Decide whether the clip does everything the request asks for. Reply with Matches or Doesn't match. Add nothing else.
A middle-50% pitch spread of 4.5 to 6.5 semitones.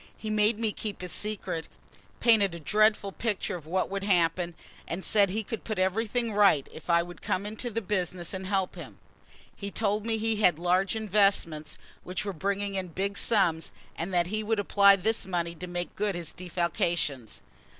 Doesn't match